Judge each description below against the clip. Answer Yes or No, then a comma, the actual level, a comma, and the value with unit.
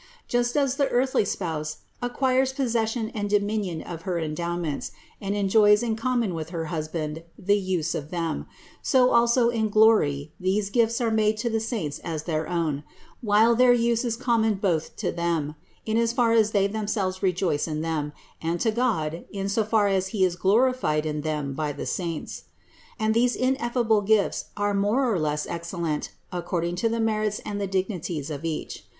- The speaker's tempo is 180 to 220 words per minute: Yes, average, 185 wpm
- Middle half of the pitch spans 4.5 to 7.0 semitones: Yes, wide, 5.5 semitones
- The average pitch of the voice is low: No, high, 200 Hz